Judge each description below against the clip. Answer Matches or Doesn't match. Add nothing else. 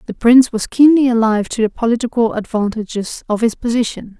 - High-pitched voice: Matches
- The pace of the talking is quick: Doesn't match